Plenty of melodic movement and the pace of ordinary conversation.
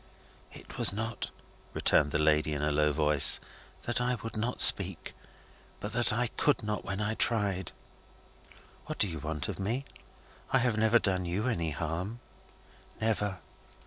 Yes: wide, 6.0 semitones; average, 160 wpm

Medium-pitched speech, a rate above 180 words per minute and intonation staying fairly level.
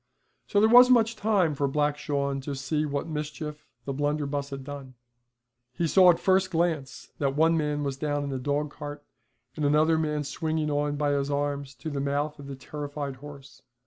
Yes: medium, 145 Hz; average, 195 wpm; narrow, 1.7 semitones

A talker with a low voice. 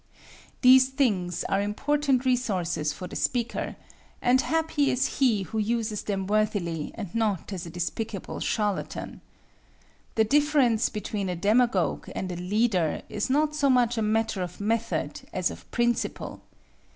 No: high, 220 Hz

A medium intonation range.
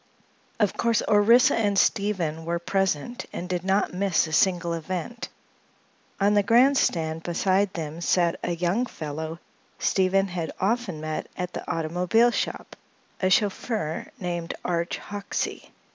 Yes: average, 3.4 semitones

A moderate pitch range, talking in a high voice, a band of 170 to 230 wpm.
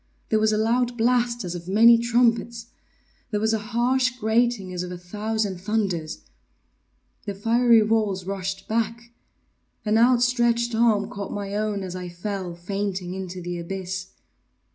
No: average, 3.7 semitones; high, 215 Hz; average, 150 wpm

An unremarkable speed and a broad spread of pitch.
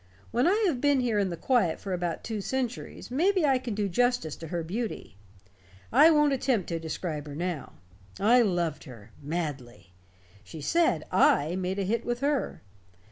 Yes: average, 180 wpm; wide, 7.6 semitones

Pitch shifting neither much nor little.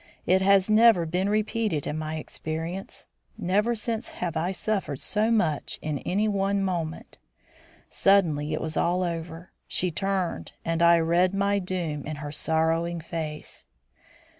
Yes: average, 3.7 semitones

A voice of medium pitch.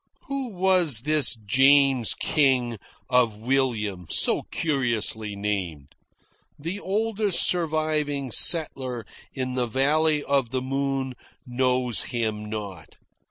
No: low, 130 Hz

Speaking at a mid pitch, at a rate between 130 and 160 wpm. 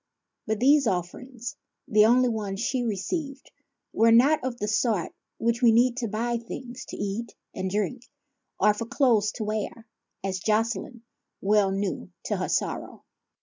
No: high, 225 Hz; average, 155 wpm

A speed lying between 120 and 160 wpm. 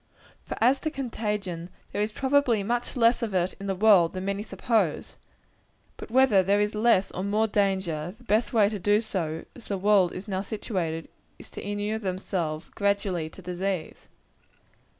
No: average, 170 wpm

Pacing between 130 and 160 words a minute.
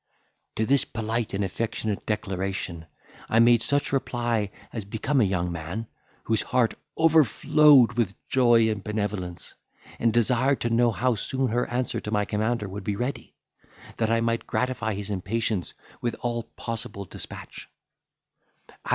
Yes: average, 150 wpm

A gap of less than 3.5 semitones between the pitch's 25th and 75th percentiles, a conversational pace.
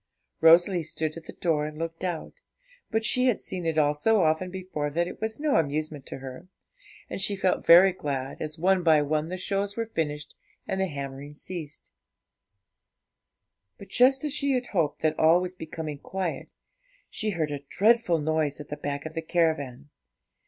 No: average, 4.1 semitones; average, 180 wpm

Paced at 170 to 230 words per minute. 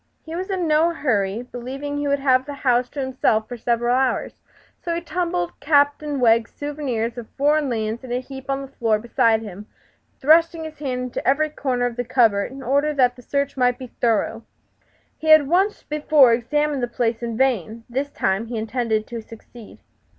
Yes: average, 195 wpm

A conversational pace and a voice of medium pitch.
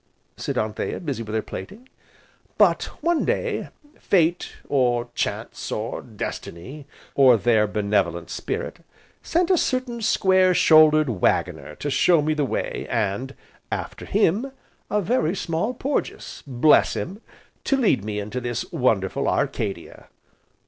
No: slow, 130 wpm; medium, 150 Hz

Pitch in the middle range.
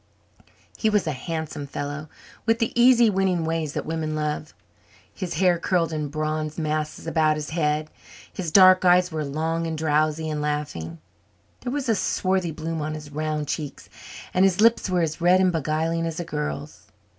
Yes: medium, 160 Hz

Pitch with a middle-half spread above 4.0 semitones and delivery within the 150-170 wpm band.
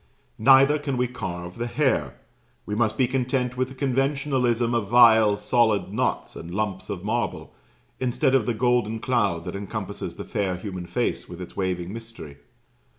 Yes: average, 4.4 semitones; average, 165 wpm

